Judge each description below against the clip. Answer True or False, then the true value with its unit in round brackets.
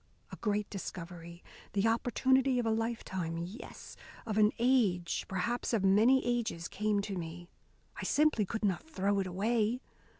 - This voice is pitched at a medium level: False (210 Hz)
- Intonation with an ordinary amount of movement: True (4.2 semitones)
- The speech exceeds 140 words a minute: True (155 wpm)